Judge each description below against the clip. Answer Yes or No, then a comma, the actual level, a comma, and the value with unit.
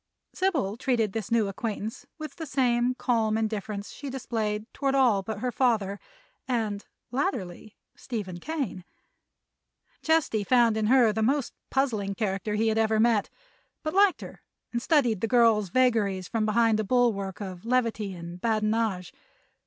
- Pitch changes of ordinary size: Yes, average, 3.4 semitones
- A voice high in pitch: Yes, high, 225 Hz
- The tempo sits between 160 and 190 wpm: No, average, 150 wpm